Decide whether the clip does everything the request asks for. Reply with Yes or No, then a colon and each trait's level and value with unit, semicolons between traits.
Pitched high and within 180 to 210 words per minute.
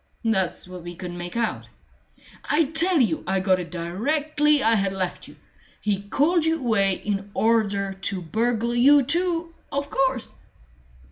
No: high, 225 Hz; average, 155 wpm